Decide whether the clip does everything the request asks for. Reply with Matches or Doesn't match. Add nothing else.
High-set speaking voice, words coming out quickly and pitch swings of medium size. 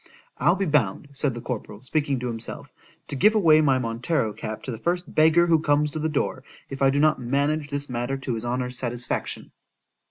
Doesn't match